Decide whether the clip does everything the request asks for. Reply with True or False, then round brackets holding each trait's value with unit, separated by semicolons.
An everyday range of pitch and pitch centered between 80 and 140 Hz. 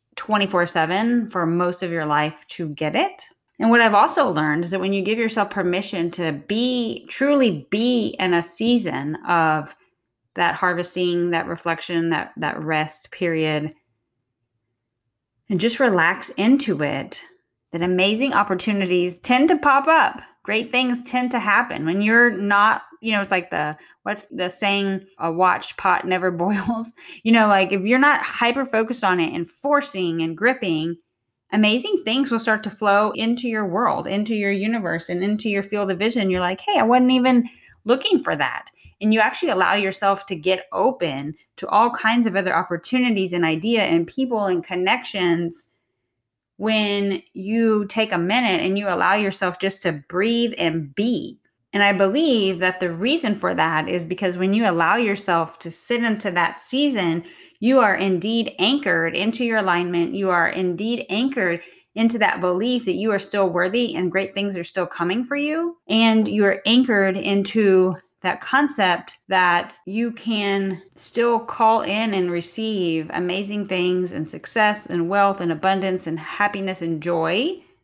False (4.6 semitones; 195 Hz)